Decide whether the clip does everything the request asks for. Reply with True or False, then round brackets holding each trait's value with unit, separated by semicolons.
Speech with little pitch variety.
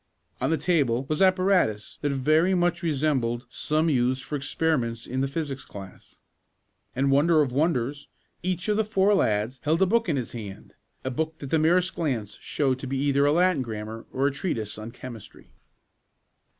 False (5.0 semitones)